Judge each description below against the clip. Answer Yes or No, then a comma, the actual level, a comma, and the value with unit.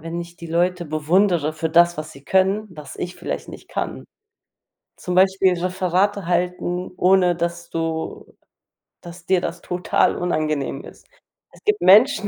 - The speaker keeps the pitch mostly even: Yes, narrow, 2.0 semitones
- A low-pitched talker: No, medium, 175 Hz